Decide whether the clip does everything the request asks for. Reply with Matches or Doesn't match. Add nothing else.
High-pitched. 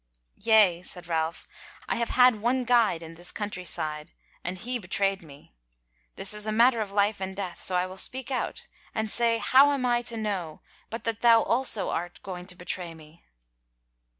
Matches